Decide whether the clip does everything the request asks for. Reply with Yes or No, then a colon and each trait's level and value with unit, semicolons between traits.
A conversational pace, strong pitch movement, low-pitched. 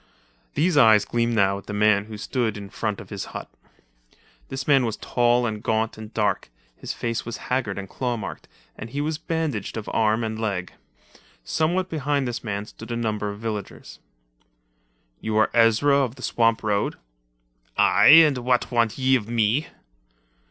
No: average, 175 wpm; average, 3.2 semitones; low, 115 Hz